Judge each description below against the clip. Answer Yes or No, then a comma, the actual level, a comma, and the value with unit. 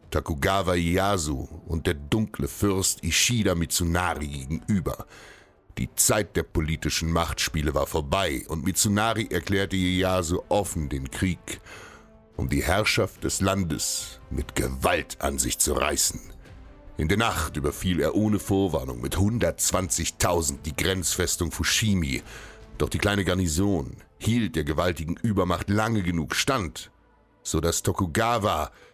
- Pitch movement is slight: No, average, 3.5 semitones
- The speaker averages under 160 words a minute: Yes, slow, 125 wpm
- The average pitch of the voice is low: Yes, very low, 90 Hz